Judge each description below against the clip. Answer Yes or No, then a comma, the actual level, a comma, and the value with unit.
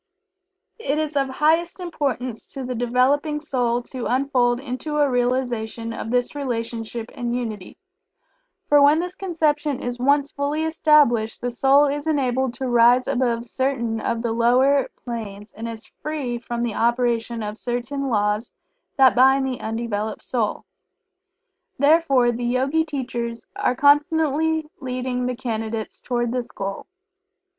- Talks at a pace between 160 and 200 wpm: No, average, 145 wpm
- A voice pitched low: No, very high, 250 Hz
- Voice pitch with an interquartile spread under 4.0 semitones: Yes, average, 3.3 semitones